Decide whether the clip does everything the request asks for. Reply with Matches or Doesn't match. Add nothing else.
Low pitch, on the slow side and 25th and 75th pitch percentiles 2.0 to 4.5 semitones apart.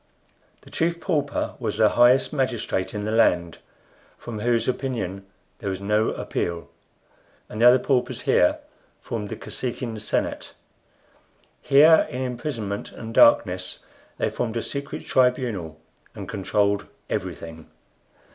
Matches